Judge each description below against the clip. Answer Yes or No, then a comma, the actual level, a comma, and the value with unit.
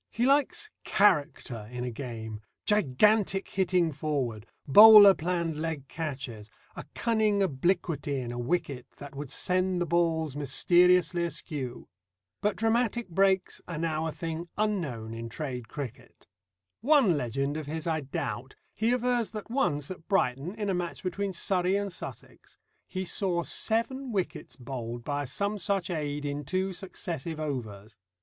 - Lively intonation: Yes, wide, 6.0 semitones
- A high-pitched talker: No, medium, 165 Hz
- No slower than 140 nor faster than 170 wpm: Yes, average, 145 wpm